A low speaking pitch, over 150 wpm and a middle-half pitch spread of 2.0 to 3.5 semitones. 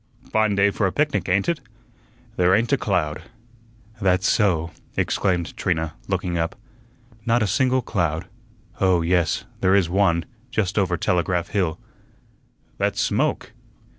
No: very low, 95 Hz; slow, 135 wpm; average, 3.1 semitones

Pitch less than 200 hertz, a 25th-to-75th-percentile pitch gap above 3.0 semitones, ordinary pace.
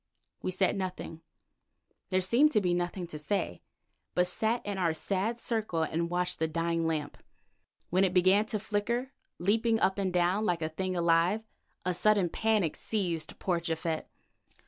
Yes: medium, 185 Hz; average, 3.5 semitones; average, 165 wpm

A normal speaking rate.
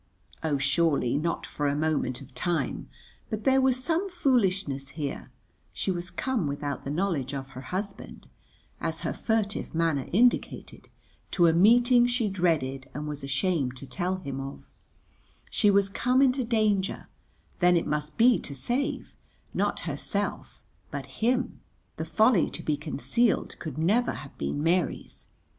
Yes: average, 150 wpm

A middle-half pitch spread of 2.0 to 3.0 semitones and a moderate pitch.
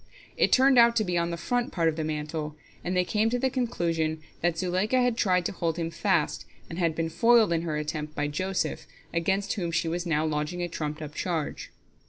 No: average, 3.8 semitones; medium, 170 Hz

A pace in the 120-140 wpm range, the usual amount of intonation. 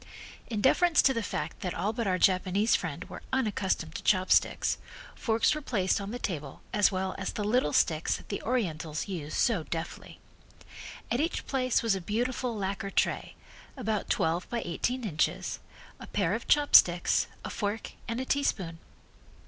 No: average, 170 wpm; average, 4.7 semitones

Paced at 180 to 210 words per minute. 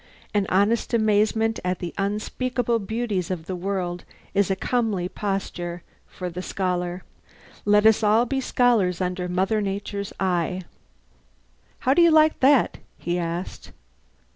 No: average, 140 wpm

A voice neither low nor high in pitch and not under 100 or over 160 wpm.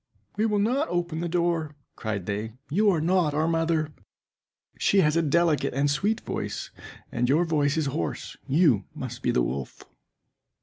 No: medium, 160 Hz; average, 170 wpm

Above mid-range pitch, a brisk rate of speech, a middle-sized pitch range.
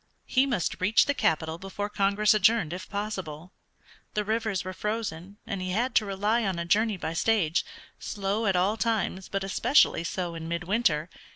No: high, 195 Hz; average, 175 wpm; average, 3.3 semitones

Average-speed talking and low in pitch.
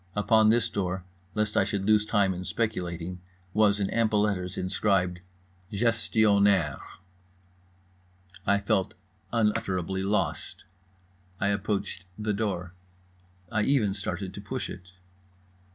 No: slow, 115 wpm; low, 100 Hz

